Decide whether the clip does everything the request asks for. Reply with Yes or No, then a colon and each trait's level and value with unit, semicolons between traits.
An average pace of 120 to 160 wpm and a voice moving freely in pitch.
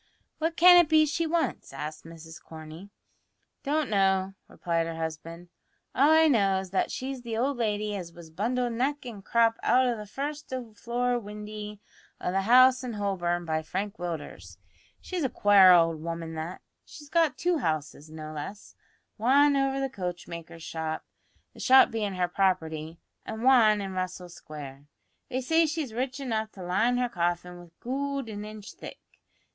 No: average, 170 wpm; wide, 6.9 semitones